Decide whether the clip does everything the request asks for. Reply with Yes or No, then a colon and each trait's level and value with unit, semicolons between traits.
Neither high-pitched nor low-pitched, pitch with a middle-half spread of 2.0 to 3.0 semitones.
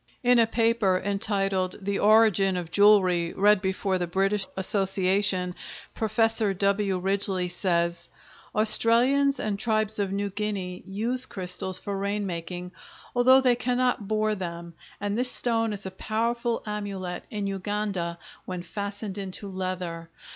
No: high, 200 Hz; average, 2.7 semitones